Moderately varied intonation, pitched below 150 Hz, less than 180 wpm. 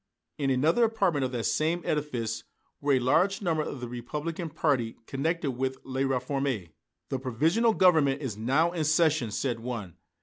Yes: average, 4.4 semitones; medium, 140 Hz; average, 165 wpm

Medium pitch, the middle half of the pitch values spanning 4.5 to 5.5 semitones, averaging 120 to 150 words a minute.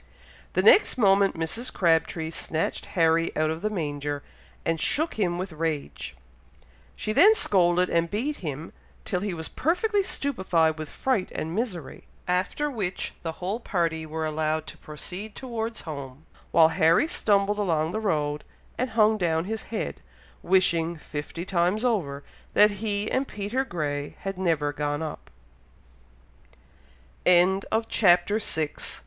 Yes: medium, 175 Hz; average, 4.9 semitones; average, 145 wpm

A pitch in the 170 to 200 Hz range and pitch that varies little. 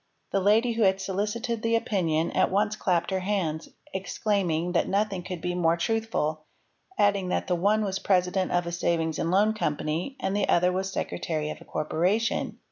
No: high, 190 Hz; average, 3.3 semitones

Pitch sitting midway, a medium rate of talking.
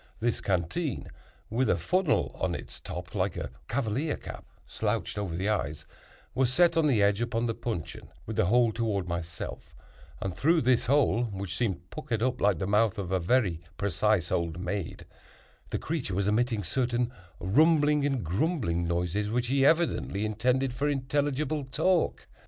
No: low, 115 Hz; average, 165 wpm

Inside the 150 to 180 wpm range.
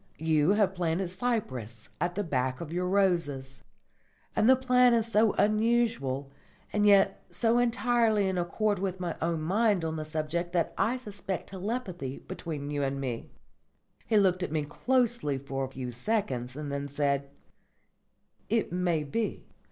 Yes: average, 160 wpm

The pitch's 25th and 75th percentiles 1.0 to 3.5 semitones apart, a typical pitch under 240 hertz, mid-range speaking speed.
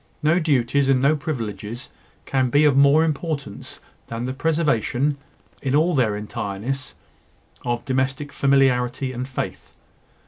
No: average, 3.0 semitones; low, 135 Hz; slow, 130 wpm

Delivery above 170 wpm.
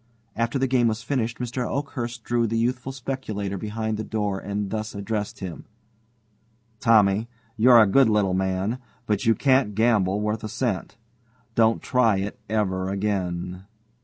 No: average, 155 wpm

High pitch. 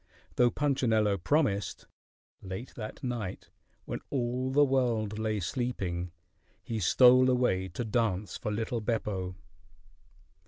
No: low, 110 Hz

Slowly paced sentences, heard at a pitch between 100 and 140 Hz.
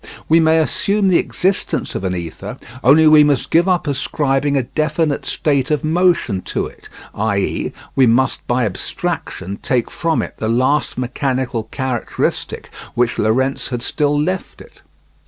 No: average, 155 wpm; low, 135 Hz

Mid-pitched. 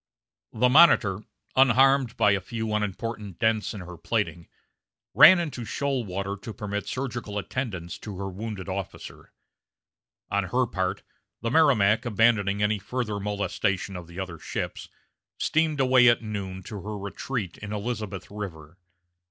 No: low, 105 Hz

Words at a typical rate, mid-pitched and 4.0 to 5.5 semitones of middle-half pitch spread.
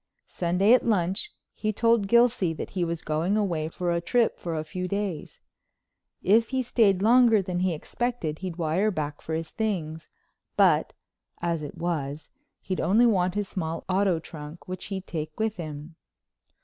Yes: average, 170 wpm; medium, 180 Hz; average, 4.4 semitones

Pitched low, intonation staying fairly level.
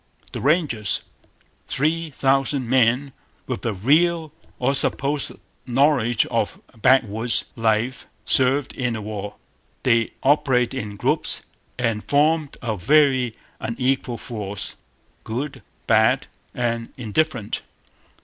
No: low, 125 Hz; average, 3.7 semitones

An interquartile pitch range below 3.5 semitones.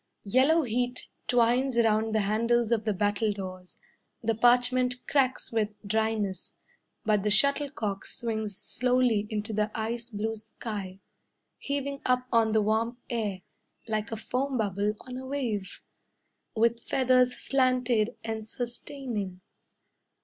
Yes: average, 2.9 semitones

